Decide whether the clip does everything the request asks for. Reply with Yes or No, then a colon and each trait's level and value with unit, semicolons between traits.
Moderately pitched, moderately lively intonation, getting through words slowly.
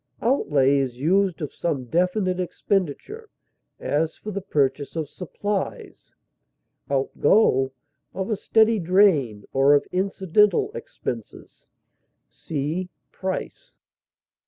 No: medium, 180 Hz; wide, 6.0 semitones; slow, 100 wpm